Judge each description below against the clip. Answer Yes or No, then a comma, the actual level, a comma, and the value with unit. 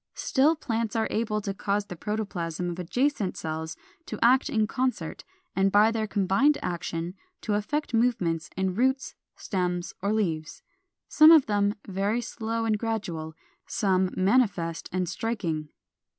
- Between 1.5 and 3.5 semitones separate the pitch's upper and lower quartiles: No, average, 4.2 semitones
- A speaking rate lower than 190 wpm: Yes, average, 145 wpm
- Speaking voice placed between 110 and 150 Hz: No, high, 205 Hz